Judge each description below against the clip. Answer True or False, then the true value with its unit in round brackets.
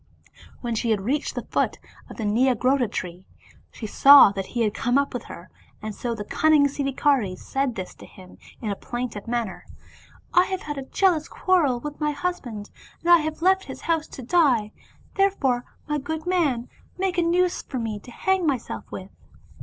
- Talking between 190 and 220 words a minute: True (195 wpm)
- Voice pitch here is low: False (265 Hz)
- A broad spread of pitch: True (6.0 semitones)